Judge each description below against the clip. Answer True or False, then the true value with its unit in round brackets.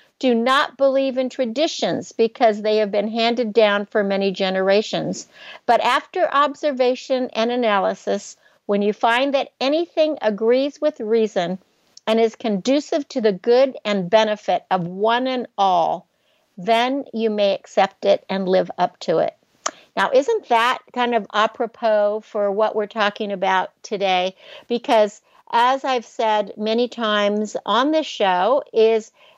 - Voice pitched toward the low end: False (225 Hz)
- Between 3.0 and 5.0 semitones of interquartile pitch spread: True (4.1 semitones)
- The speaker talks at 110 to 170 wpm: True (145 wpm)